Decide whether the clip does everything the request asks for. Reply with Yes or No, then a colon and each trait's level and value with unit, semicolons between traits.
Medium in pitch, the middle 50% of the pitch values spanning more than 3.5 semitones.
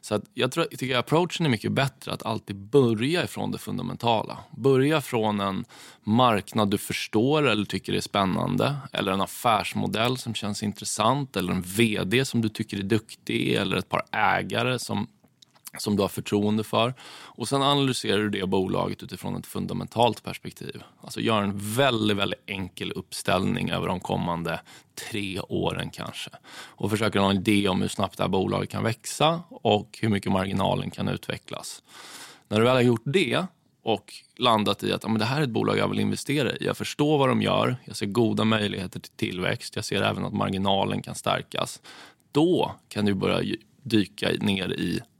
No: low, 110 Hz; average, 4.1 semitones